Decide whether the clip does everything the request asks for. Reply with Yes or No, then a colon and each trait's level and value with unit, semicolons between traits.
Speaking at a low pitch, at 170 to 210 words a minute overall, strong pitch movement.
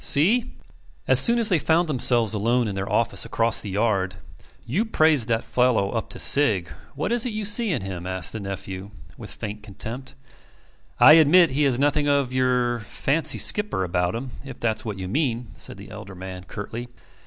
Yes: low, 120 Hz; average, 190 wpm; wide, 6.5 semitones